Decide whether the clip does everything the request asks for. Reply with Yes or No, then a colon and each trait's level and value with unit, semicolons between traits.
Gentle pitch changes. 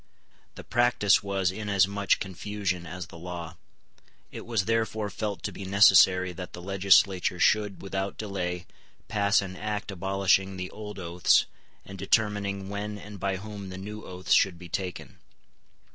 Yes: narrow, 2.0 semitones